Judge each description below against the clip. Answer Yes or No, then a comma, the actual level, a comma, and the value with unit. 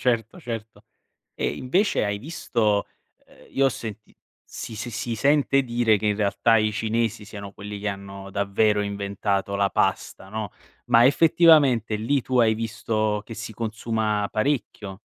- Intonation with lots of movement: No, narrow, 2.6 semitones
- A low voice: Yes, low, 110 Hz